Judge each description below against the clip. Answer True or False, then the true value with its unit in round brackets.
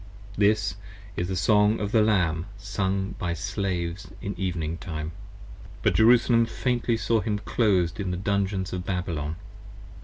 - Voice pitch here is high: False (95 Hz)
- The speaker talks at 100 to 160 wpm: True (145 wpm)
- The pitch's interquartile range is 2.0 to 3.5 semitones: True (3.1 semitones)